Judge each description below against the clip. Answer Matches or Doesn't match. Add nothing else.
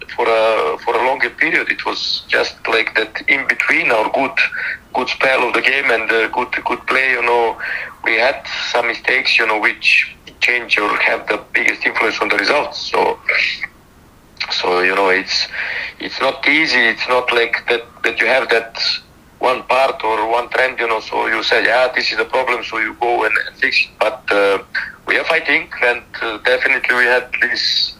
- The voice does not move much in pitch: Matches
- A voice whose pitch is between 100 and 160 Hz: Matches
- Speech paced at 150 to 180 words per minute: Doesn't match